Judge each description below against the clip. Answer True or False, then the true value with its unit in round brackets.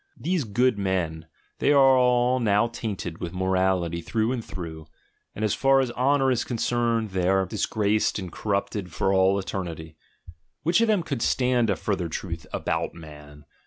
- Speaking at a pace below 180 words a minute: True (170 wpm)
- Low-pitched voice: True (100 Hz)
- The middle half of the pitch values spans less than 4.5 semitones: False (5.6 semitones)